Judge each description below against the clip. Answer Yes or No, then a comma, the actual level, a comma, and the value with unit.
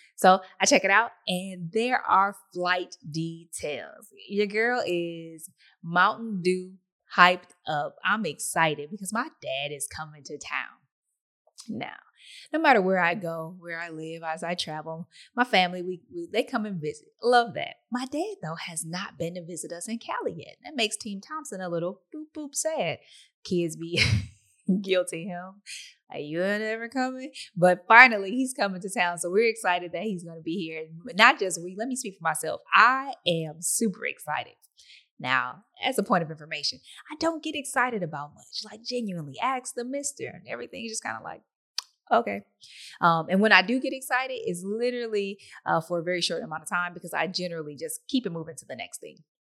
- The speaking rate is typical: Yes, average, 195 wpm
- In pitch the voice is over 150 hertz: Yes, medium, 185 Hz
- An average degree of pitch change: No, wide, 6.2 semitones